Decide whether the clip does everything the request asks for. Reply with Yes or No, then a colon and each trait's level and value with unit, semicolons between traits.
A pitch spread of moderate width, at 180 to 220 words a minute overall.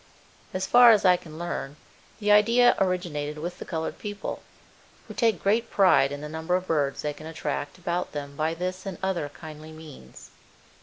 Yes: average, 4.0 semitones; average, 185 wpm